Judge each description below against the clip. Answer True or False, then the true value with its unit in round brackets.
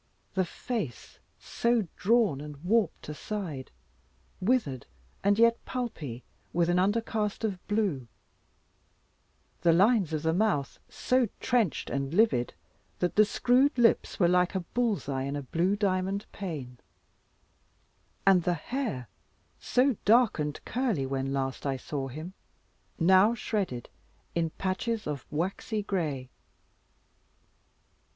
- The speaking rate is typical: False (125 wpm)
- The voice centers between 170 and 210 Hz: True (185 Hz)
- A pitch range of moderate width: False (6.9 semitones)